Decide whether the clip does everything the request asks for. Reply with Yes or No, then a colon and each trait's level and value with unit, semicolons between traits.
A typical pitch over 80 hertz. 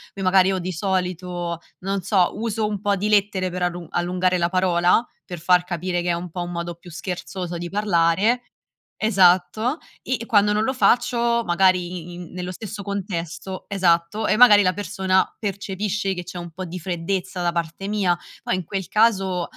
Yes: medium, 185 Hz